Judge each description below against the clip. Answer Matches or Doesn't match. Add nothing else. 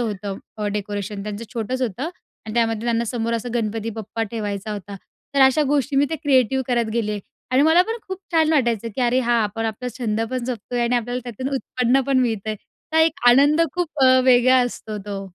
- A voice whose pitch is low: Doesn't match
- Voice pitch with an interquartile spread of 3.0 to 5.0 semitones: Matches